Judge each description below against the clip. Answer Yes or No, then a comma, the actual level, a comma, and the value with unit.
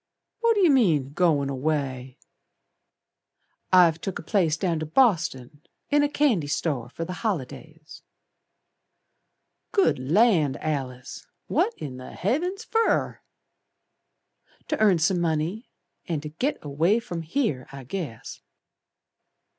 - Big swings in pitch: Yes, wide, 7.2 semitones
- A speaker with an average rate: No, slow, 120 wpm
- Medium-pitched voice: Yes, medium, 165 Hz